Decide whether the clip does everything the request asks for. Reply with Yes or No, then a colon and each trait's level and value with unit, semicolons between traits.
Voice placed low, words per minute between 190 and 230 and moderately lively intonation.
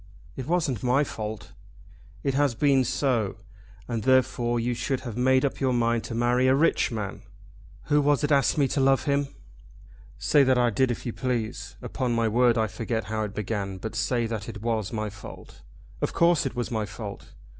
Yes: low, 120 Hz; average, 200 wpm; average, 3.2 semitones